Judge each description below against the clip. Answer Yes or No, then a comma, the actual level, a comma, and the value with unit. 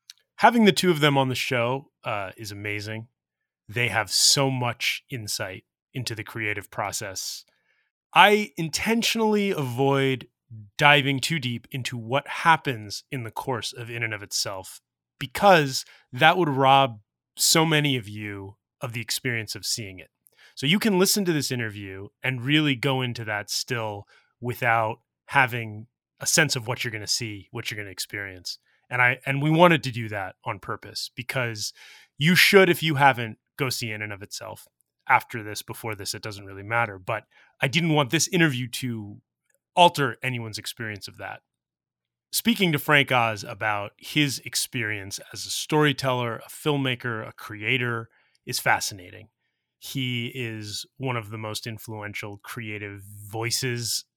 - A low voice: Yes, low, 120 Hz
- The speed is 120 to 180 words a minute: Yes, average, 160 wpm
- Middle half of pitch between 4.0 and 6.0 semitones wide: Yes, average, 4.5 semitones